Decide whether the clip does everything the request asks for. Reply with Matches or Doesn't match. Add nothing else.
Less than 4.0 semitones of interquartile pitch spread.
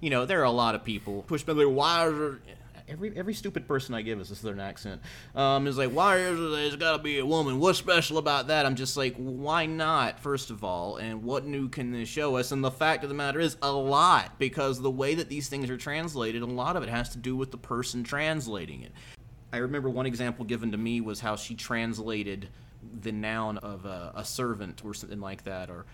Doesn't match